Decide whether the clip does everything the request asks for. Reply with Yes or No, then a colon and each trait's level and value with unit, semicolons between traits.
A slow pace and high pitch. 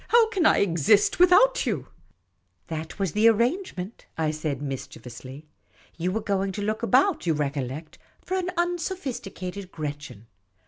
No: average, 165 wpm; high, 195 Hz